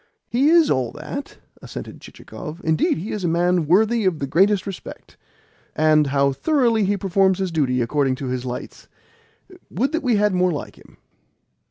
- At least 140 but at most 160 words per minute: No, average, 175 wpm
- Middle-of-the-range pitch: Yes, medium, 180 Hz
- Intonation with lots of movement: Yes, wide, 5.8 semitones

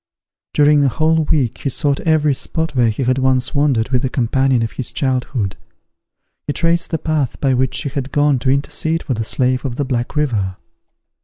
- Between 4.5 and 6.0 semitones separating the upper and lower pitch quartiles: No, average, 3.0 semitones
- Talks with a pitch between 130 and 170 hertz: Yes, low, 135 Hz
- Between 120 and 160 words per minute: No, average, 200 wpm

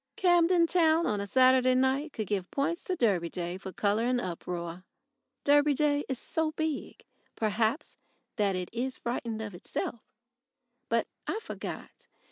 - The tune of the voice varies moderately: No, wide, 6.7 semitones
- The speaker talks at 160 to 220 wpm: No, average, 150 wpm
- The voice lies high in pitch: Yes, high, 245 Hz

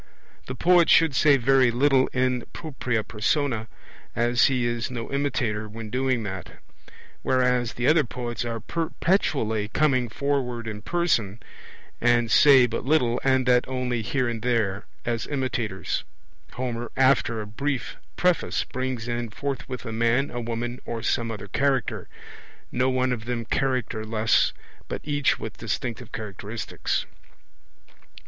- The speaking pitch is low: Yes, low, 120 Hz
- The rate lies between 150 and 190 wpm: No, average, 140 wpm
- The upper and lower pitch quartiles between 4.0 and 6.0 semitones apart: No, average, 2.7 semitones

